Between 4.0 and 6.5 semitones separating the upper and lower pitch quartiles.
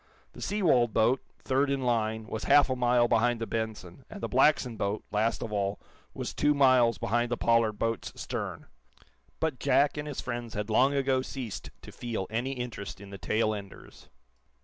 No: average, 3.3 semitones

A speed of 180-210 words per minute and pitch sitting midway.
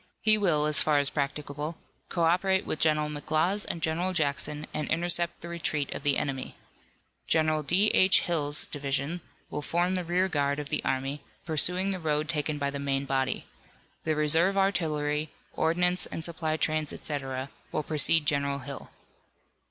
No: average, 165 wpm; medium, 155 Hz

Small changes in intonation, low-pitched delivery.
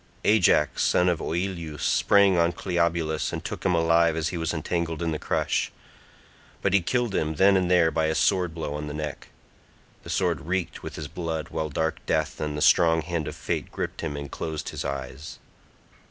Yes: narrow, 2.3 semitones; very low, 80 Hz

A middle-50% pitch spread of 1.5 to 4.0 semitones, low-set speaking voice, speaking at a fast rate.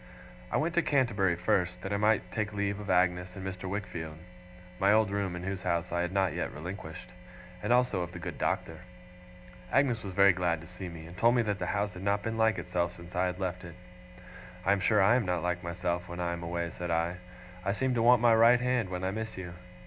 Yes: average, 3.2 semitones; very low, 95 Hz; fast, 240 wpm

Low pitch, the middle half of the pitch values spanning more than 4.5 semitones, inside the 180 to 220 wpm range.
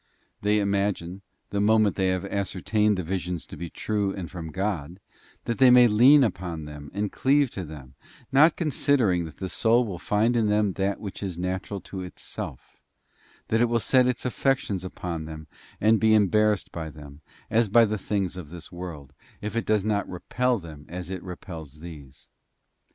No: low, 100 Hz; average, 3.9 semitones; average, 185 wpm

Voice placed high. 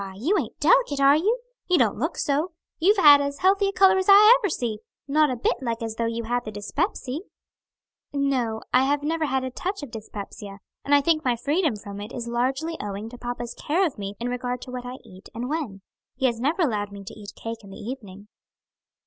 Yes: very high, 255 Hz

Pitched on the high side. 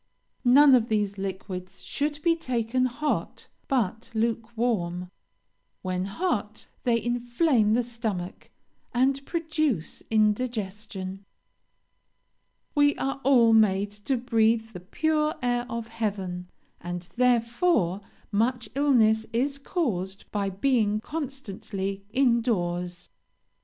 Yes: high, 230 Hz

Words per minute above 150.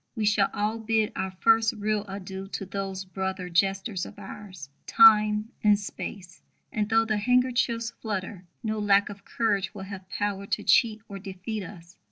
Yes: average, 170 wpm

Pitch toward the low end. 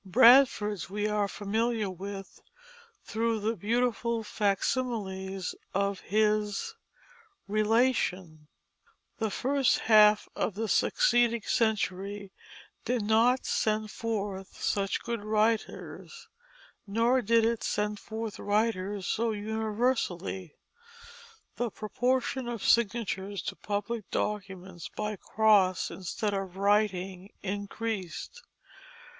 No: high, 210 Hz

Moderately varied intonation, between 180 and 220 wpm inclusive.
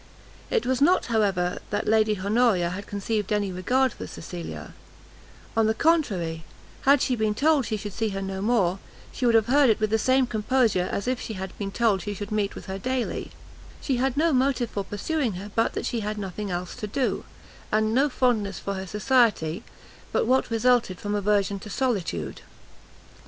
Yes: average, 4.1 semitones; average, 195 wpm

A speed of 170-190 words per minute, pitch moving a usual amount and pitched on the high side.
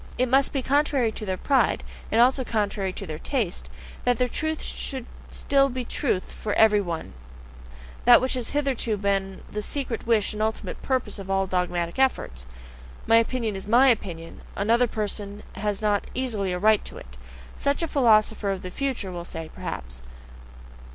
Yes: average, 175 wpm; average, 4.8 semitones; high, 215 Hz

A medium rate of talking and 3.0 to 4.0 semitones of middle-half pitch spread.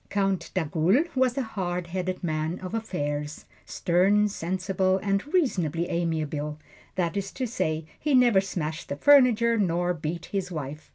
No: average, 150 wpm; average, 4.4 semitones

